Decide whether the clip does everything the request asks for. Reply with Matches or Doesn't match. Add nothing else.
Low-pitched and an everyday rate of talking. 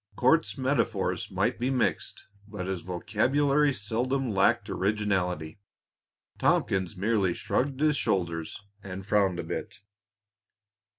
Doesn't match